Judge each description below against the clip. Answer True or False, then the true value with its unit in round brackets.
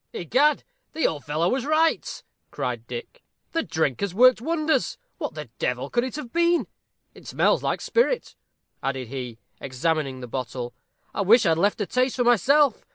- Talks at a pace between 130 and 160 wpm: False (170 wpm)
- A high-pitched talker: True (225 Hz)